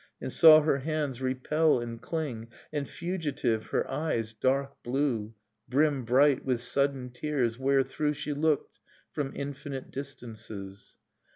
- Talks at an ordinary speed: No, slow, 125 wpm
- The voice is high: No, low, 135 Hz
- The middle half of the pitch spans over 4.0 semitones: No, average, 3.4 semitones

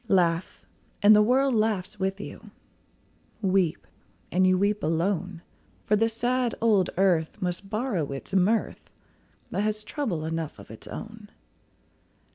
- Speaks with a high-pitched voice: Yes, high, 195 Hz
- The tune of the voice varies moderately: Yes, average, 3.5 semitones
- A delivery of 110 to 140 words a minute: Yes, slow, 135 wpm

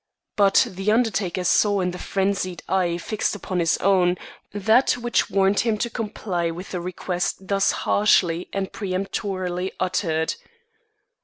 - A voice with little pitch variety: Yes, narrow, 2.2 semitones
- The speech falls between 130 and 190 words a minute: Yes, average, 140 wpm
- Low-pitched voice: No, high, 190 Hz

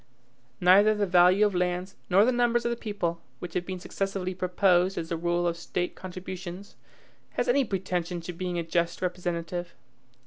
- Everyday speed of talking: Yes, average, 175 wpm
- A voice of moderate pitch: Yes, medium, 180 Hz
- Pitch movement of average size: No, narrow, 2.0 semitones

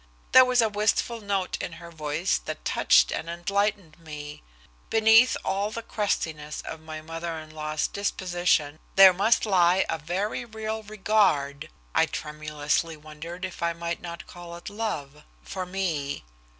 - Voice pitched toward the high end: No, medium, 175 Hz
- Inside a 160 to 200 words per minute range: No, average, 150 wpm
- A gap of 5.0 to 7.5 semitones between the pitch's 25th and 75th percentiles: No, average, 4.6 semitones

